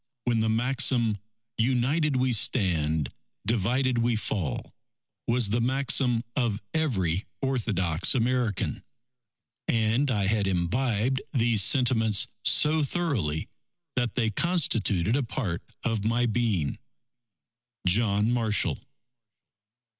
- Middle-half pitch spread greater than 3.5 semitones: Yes, average, 4.0 semitones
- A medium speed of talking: No, slow, 100 wpm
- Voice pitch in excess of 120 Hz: No, low, 115 Hz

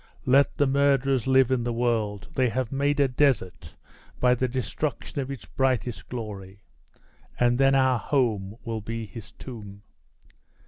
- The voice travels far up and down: No, average, 3.4 semitones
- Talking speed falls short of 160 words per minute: Yes, average, 150 wpm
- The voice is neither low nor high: No, low, 125 Hz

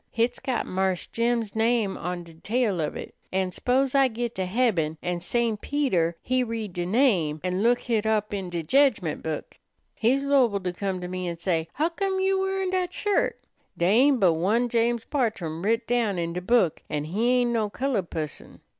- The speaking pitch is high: Yes, high, 220 Hz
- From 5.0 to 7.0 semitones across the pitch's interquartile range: Yes, wide, 5.6 semitones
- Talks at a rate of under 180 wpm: No, average, 195 wpm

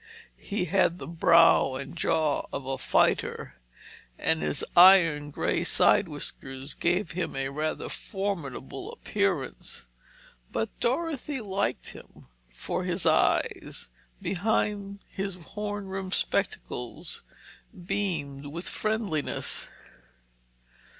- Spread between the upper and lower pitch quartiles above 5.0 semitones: Yes, wide, 5.4 semitones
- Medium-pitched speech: Yes, medium, 175 Hz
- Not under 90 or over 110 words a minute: Yes, slow, 105 wpm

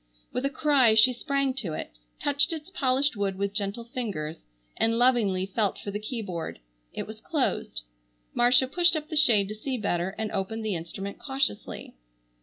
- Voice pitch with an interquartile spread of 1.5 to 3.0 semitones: No, average, 5.1 semitones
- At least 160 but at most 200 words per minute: Yes, average, 175 wpm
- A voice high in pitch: Yes, high, 225 Hz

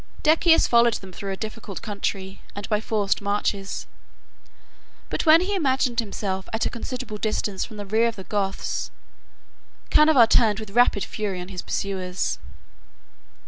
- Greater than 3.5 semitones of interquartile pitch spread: No, average, 3.2 semitones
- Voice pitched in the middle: No, high, 210 Hz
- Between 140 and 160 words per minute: Yes, average, 155 wpm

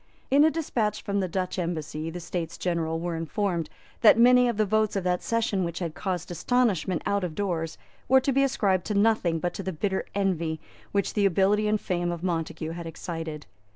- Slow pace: No, fast, 205 wpm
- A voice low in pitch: No, medium, 185 Hz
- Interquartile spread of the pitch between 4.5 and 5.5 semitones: No, average, 4.0 semitones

